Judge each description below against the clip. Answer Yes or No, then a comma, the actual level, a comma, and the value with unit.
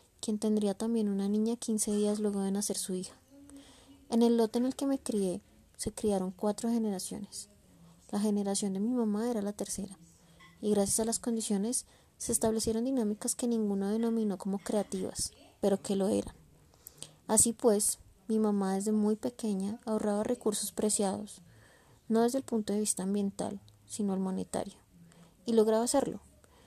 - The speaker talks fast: No, average, 160 wpm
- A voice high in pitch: Yes, high, 210 Hz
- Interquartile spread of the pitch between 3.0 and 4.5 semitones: No, narrow, 2.5 semitones